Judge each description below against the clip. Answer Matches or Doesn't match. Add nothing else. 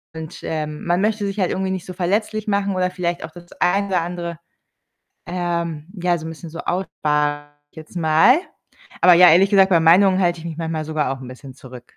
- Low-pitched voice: Doesn't match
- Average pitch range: Matches